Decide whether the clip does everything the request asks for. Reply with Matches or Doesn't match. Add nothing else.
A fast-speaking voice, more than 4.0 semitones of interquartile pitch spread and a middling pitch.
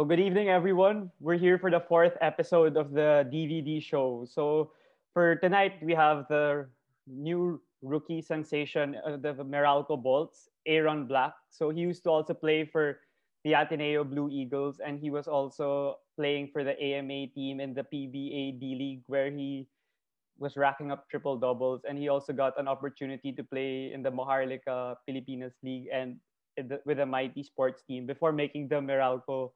Doesn't match